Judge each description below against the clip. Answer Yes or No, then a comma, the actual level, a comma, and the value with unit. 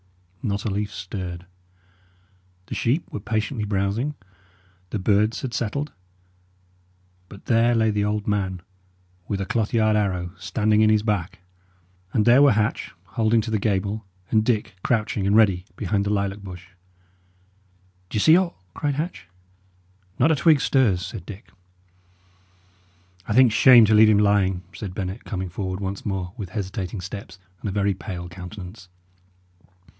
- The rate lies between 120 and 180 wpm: Yes, average, 155 wpm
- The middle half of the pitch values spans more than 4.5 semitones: No, narrow, 2.6 semitones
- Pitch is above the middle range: No, low, 105 Hz